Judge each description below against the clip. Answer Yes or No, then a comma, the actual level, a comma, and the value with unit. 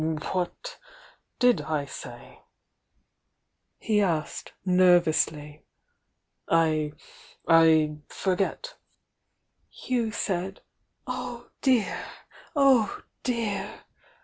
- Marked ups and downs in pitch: Yes, wide, 6.7 semitones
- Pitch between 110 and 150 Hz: No, medium, 185 Hz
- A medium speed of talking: No, slow, 70 wpm